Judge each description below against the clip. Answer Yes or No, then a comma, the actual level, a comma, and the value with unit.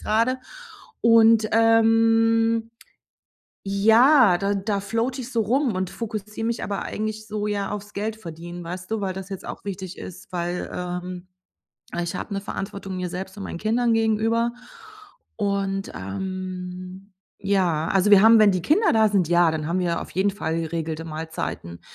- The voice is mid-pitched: No, high, 200 Hz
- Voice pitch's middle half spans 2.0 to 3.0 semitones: No, average, 3.6 semitones